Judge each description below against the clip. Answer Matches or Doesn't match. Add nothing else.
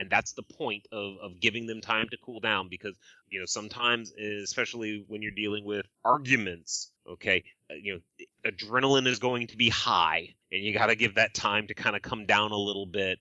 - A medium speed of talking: Doesn't match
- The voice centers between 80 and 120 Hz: Matches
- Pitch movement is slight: Matches